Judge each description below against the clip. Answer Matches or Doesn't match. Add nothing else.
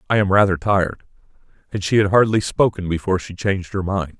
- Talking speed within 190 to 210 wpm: Matches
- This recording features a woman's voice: Doesn't match